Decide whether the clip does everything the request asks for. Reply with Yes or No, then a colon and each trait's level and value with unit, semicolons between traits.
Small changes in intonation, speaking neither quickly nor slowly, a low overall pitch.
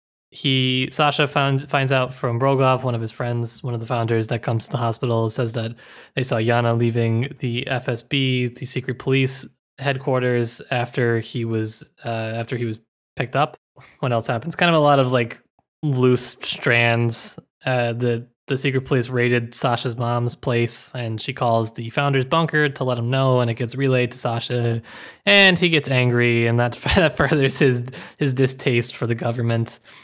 Yes: narrow, 2.3 semitones; average, 180 wpm; low, 125 Hz